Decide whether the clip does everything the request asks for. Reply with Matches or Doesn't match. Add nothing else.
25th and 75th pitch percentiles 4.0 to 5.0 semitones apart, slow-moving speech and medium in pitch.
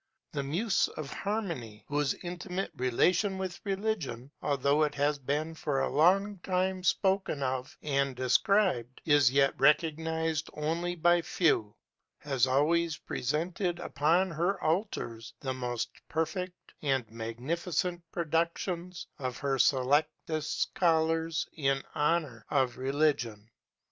Matches